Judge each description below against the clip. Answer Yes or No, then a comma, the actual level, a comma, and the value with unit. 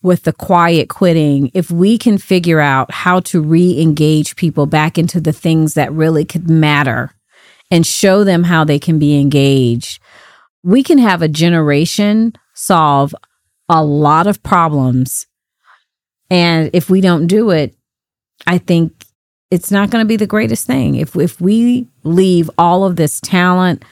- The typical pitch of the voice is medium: Yes, medium, 170 Hz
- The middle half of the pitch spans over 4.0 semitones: No, average, 3.3 semitones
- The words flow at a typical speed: Yes, average, 160 wpm